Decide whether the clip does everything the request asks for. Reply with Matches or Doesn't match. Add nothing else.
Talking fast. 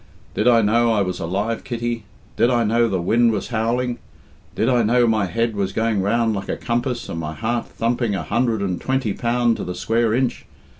Matches